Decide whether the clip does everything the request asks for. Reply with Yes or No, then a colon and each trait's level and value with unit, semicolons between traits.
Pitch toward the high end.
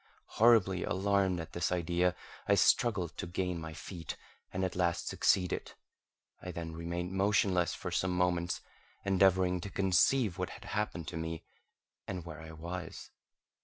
No: very low, 90 Hz